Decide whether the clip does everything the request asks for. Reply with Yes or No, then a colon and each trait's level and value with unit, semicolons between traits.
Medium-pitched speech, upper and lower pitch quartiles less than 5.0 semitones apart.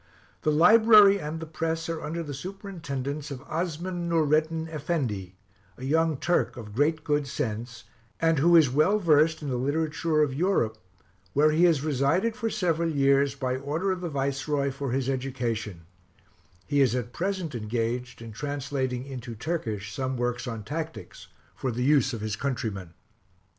Yes: medium, 145 Hz; average, 4.5 semitones